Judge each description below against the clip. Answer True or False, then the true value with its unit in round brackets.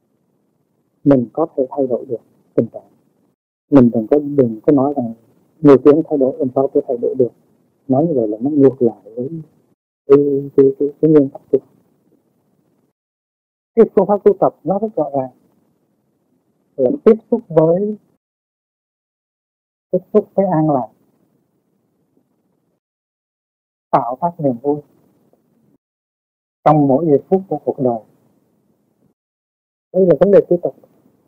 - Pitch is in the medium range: True (145 Hz)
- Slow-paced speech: True (145 wpm)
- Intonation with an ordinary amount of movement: True (4.2 semitones)